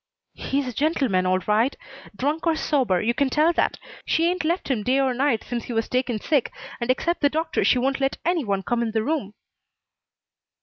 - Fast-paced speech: Yes, fast, 210 wpm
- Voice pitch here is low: No, very high, 260 Hz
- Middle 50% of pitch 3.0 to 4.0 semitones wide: No, average, 5.0 semitones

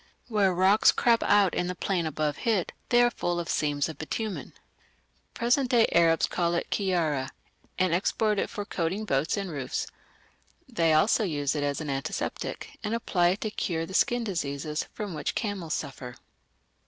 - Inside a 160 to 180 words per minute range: Yes, average, 175 wpm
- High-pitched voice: No, medium, 175 Hz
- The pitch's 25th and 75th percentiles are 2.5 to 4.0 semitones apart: No, average, 5.2 semitones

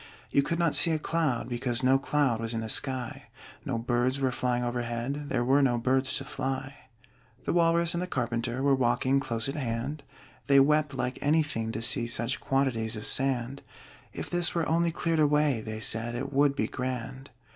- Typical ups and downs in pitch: Yes, average, 3.3 semitones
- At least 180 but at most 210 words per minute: Yes, average, 190 wpm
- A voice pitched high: No, low, 130 Hz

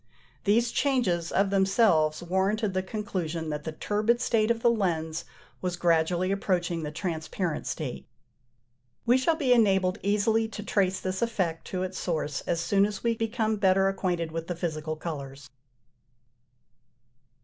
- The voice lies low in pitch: No, medium, 185 Hz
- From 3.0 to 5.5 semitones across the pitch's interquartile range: Yes, average, 4.5 semitones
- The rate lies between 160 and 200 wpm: No, average, 150 wpm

